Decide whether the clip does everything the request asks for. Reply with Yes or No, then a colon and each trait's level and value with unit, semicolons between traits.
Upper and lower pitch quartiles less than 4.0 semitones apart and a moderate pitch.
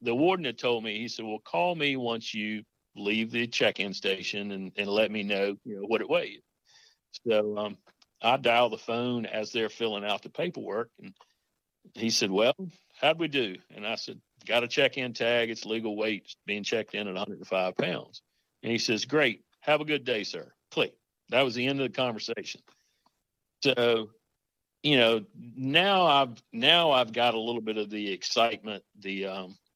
No: average, 3.2 semitones; low, 115 Hz